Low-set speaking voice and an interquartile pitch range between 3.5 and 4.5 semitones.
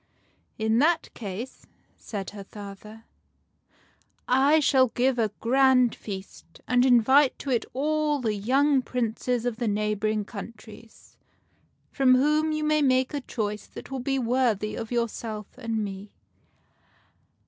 No: high, 240 Hz; average, 3.8 semitones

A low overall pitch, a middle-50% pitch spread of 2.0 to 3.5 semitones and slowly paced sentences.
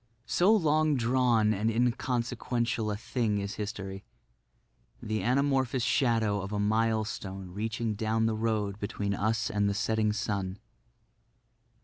Yes: low, 110 Hz; narrow, 2.6 semitones; slow, 120 wpm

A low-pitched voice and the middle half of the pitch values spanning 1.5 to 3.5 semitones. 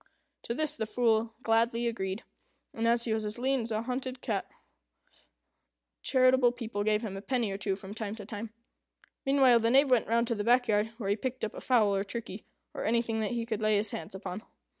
No: high, 225 Hz; narrow, 2.5 semitones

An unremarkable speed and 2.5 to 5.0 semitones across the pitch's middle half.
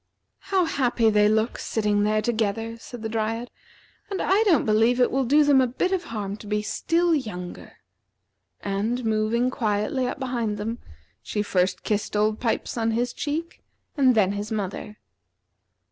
Yes: average, 165 wpm; average, 3.3 semitones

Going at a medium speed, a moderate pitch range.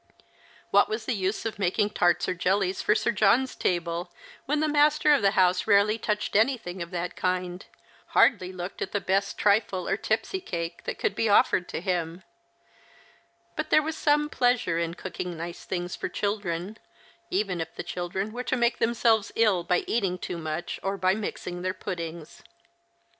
Yes: average, 180 wpm; average, 3.8 semitones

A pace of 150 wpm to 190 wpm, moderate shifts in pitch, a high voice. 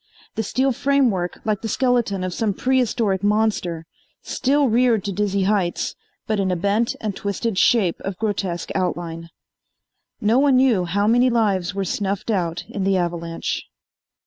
Yes: average, 155 wpm; average, 3.9 semitones; high, 205 Hz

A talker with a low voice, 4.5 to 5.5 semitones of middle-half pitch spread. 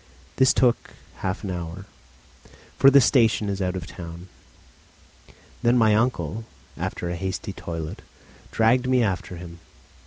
Yes: low, 100 Hz; average, 5.2 semitones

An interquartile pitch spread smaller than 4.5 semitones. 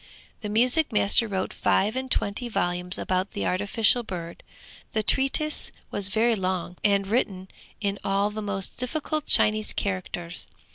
Yes: average, 3.6 semitones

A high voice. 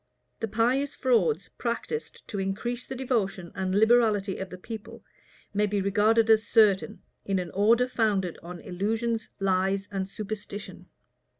Yes: high, 210 Hz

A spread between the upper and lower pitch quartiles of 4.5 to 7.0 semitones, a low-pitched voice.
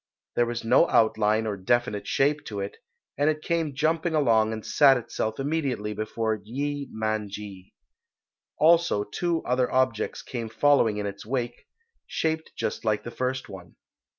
Yes: average, 5.1 semitones; low, 120 Hz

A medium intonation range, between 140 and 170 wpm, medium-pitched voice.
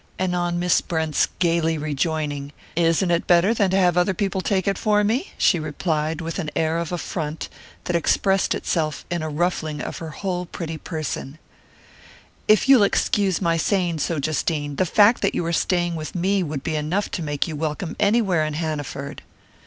No: average, 3.2 semitones; average, 185 wpm; medium, 170 Hz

